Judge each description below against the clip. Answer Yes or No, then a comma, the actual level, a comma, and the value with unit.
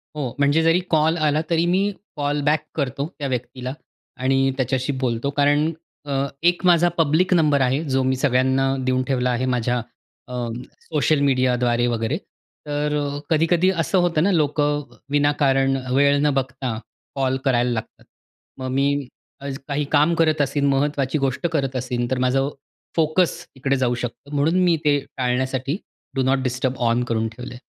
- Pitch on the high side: No, medium, 140 Hz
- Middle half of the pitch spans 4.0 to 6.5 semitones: No, average, 2.7 semitones